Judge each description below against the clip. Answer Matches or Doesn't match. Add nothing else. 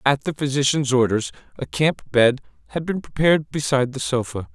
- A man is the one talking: Matches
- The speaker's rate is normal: Matches